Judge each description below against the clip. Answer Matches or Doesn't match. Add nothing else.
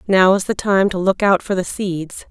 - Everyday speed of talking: Doesn't match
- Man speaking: Doesn't match